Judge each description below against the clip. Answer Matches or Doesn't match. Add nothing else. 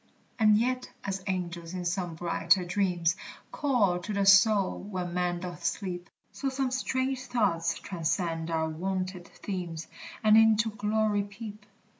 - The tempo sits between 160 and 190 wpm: Doesn't match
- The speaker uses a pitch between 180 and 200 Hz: Matches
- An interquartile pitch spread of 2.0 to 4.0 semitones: Matches